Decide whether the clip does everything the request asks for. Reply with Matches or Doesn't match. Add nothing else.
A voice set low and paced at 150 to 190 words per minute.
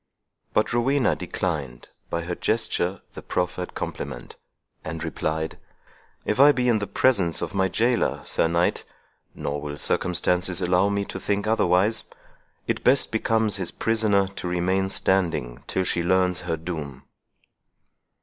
Doesn't match